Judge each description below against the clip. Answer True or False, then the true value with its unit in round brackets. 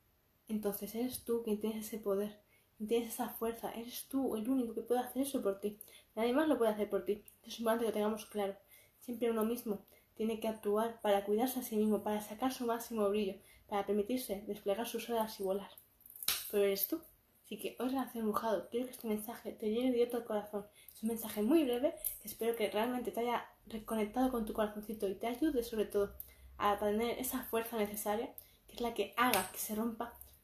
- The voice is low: False (225 Hz)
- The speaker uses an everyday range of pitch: False (2.3 semitones)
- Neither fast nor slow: False (215 wpm)